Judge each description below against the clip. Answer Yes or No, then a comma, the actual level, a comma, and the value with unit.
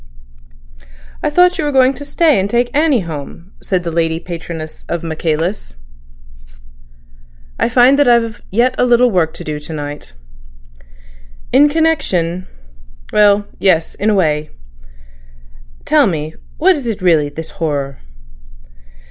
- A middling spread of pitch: No, wide, 7.6 semitones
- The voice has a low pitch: No, high, 190 Hz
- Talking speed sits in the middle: No, slow, 130 wpm